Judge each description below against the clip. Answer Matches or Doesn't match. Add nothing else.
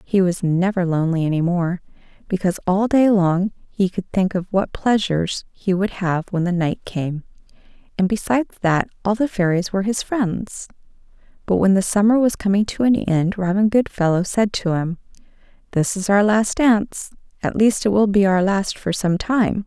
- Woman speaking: Matches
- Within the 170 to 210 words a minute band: Matches